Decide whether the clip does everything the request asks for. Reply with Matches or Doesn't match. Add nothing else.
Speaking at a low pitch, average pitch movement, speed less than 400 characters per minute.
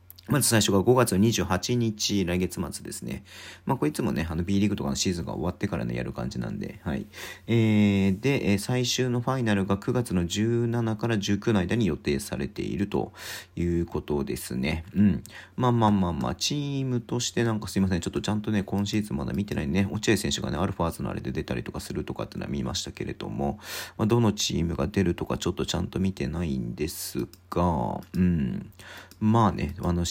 Doesn't match